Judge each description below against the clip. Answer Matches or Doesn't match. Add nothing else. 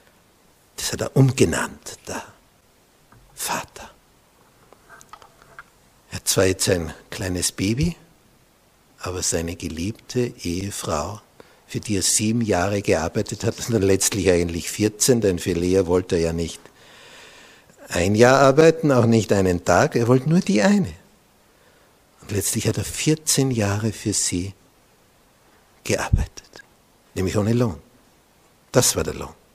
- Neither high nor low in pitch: Doesn't match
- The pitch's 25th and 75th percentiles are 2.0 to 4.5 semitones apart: Doesn't match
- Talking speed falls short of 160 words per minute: Matches